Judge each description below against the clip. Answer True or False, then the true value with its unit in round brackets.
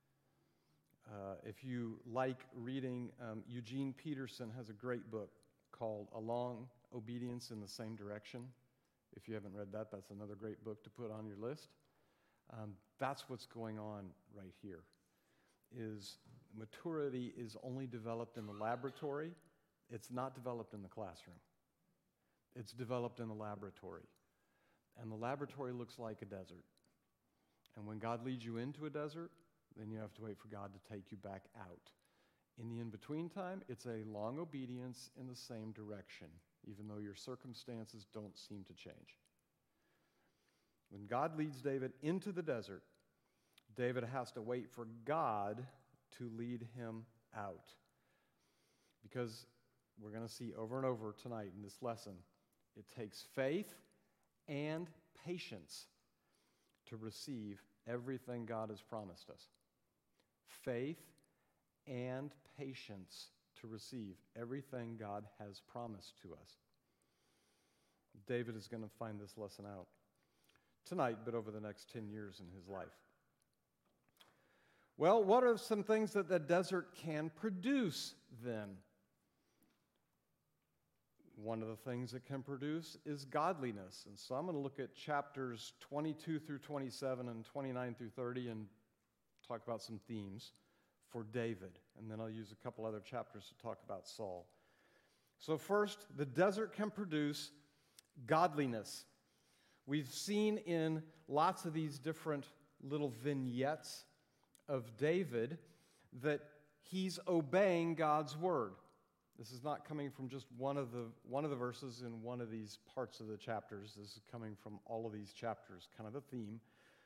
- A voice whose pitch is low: True (120 Hz)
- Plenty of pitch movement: False (4.7 semitones)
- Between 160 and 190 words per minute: False (150 wpm)